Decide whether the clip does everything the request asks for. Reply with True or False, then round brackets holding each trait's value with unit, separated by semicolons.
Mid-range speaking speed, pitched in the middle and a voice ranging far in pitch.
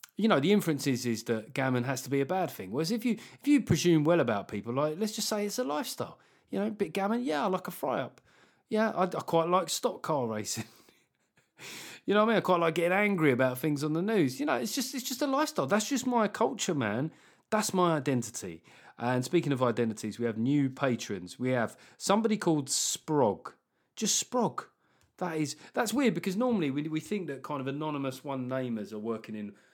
False (225 wpm; 165 Hz; 8.3 semitones)